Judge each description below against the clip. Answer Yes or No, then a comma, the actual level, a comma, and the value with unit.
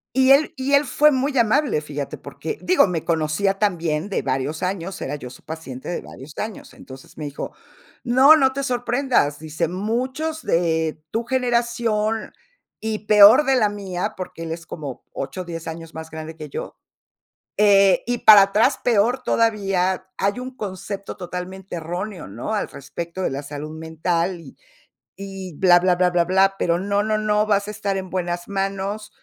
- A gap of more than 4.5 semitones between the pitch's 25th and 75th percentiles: Yes, average, 4.9 semitones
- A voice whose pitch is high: Yes, high, 195 Hz